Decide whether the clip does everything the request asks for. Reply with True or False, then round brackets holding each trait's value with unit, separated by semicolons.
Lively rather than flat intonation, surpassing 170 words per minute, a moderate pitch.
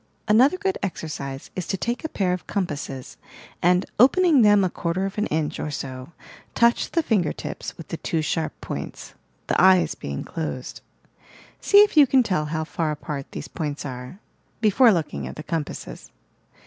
True (6.5 semitones; 185 wpm; 175 Hz)